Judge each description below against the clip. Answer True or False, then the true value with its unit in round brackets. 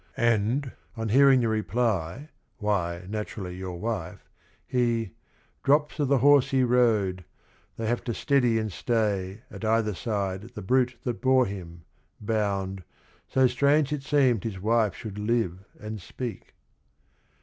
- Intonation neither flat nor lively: True (4.1 semitones)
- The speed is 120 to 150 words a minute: True (145 wpm)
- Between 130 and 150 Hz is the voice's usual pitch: False (115 Hz)